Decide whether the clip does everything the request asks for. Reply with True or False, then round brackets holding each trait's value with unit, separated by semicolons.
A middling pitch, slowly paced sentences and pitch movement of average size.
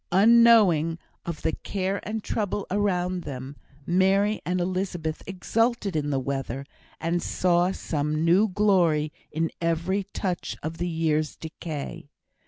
True (175 Hz; 130 wpm; 3.8 semitones)